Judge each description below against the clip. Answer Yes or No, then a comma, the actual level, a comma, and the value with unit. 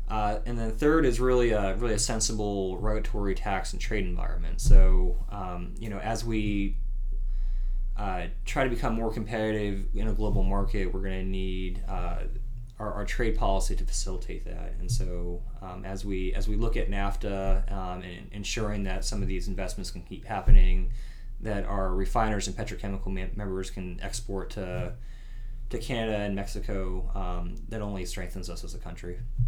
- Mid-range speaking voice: No, low, 100 Hz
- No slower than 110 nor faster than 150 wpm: No, average, 175 wpm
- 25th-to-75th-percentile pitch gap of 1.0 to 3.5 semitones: Yes, average, 2.9 semitones